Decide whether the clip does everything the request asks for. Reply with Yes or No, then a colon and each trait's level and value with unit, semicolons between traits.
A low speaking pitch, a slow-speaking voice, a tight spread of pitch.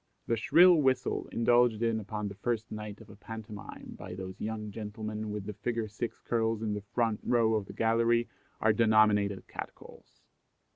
No: low, 110 Hz; average, 180 wpm; narrow, 1.8 semitones